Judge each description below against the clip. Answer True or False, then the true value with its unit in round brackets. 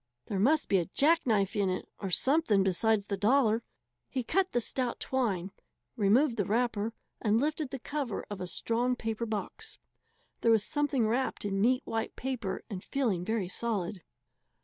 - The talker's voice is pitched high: True (225 Hz)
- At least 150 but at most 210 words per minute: True (170 wpm)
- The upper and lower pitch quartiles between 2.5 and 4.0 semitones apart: False (4.5 semitones)